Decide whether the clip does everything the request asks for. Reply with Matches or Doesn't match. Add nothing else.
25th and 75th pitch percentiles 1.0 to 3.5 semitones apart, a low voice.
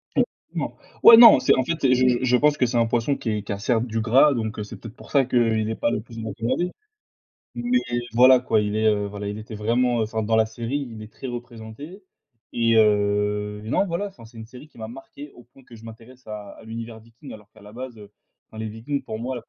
Matches